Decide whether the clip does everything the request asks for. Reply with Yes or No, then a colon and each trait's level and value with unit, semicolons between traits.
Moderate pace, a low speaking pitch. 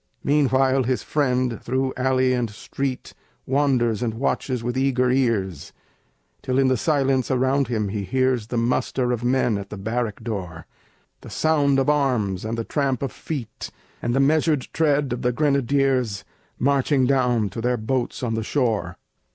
Yes: average, 165 wpm; low, 125 Hz